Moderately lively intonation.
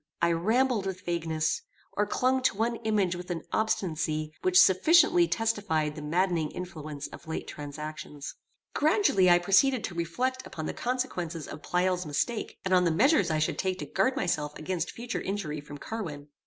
No: wide, 6.2 semitones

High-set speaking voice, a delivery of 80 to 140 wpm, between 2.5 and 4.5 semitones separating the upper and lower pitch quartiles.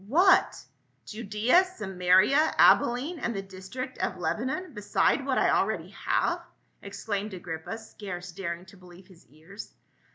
No: high, 200 Hz; slow, 135 wpm; average, 4.9 semitones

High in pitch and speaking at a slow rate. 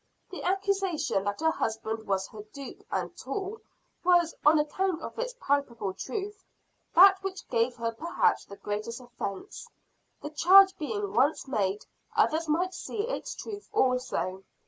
No: very high, 315 Hz; average, 145 wpm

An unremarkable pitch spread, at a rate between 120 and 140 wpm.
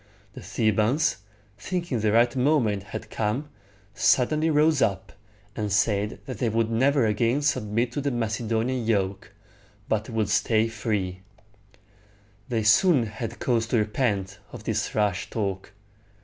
Yes: average, 3.3 semitones; slow, 135 wpm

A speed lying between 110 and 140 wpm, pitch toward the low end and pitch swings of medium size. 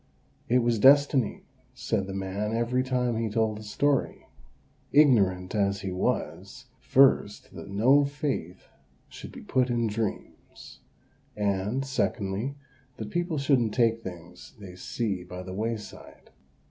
Yes: slow, 135 wpm; low, 110 Hz; average, 4.6 semitones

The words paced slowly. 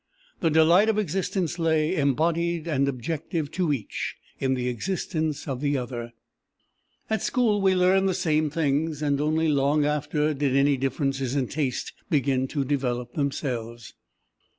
No: average, 150 wpm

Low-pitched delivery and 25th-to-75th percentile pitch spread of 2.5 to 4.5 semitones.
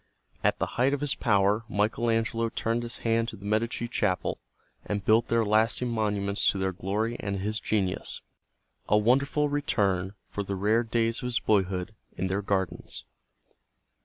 Yes: low, 110 Hz; average, 2.8 semitones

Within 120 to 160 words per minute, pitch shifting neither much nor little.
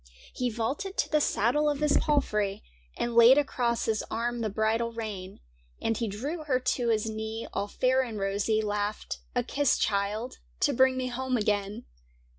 No: average, 185 wpm; average, 3.3 semitones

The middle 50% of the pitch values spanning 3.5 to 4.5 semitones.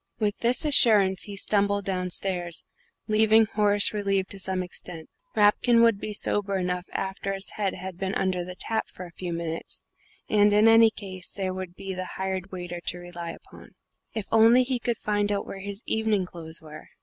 No: narrow, 2.5 semitones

